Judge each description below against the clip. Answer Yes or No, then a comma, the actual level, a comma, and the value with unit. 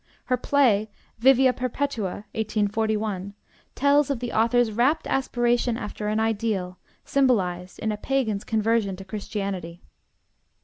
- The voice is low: No, high, 220 Hz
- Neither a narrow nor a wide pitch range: Yes, average, 3.7 semitones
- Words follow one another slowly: Yes, slow, 120 wpm